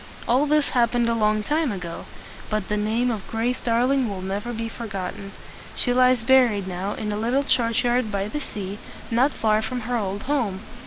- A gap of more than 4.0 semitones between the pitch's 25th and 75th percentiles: No, average, 3.2 semitones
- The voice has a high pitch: Yes, high, 230 Hz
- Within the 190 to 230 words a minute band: Yes, average, 195 wpm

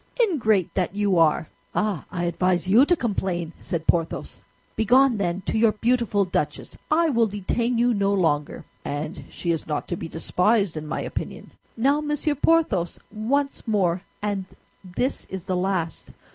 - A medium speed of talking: Yes, average, 160 wpm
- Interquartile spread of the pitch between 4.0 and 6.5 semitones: Yes, average, 5.3 semitones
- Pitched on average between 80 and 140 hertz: No, high, 200 Hz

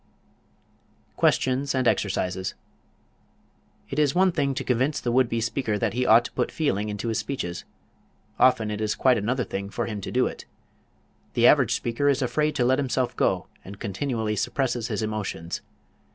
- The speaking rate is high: No, average, 175 wpm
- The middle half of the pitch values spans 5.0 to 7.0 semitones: No, average, 3.8 semitones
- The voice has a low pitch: Yes, low, 120 Hz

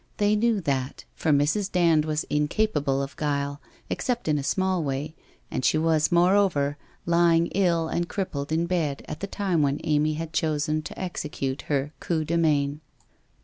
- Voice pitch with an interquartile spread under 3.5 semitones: Yes, average, 3.1 semitones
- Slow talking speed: No, average, 175 wpm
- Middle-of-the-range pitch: Yes, medium, 155 Hz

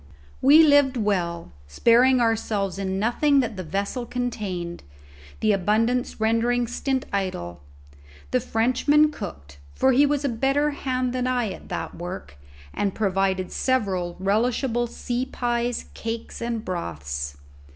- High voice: Yes, high, 225 Hz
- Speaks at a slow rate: Yes, slow, 130 wpm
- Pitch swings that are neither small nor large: Yes, average, 5.0 semitones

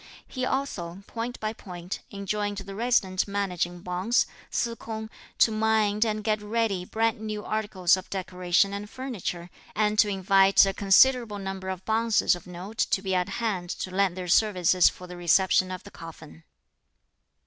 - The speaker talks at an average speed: Yes, average, 165 wpm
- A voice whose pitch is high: Yes, high, 200 Hz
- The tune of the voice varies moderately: Yes, average, 3.0 semitones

